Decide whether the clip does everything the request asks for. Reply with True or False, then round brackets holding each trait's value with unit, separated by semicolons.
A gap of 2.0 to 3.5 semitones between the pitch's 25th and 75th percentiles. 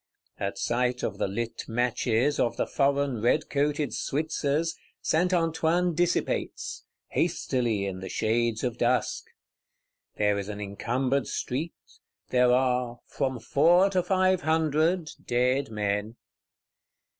False (5.2 semitones)